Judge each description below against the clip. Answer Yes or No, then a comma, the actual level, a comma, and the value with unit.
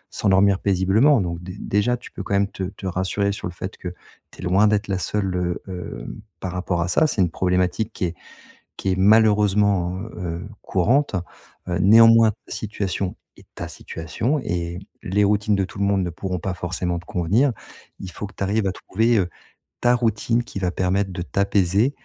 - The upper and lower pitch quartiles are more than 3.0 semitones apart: No, average, 2.7 semitones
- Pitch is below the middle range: Yes, very low, 95 Hz